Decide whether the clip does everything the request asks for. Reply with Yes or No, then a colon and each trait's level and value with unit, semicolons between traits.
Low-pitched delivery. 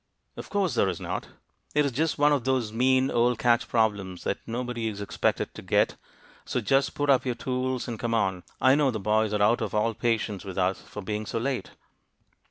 Yes: low, 115 Hz